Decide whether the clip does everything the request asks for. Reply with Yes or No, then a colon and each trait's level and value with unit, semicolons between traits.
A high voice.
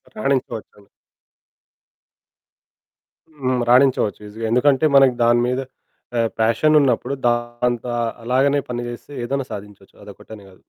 No: low, 120 Hz